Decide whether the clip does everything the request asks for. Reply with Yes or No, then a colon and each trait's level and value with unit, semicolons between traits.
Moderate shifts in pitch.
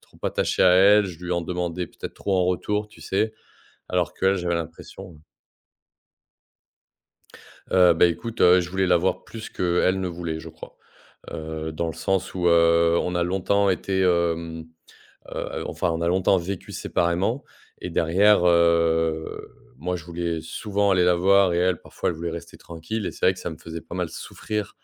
No: narrow, 2.3 semitones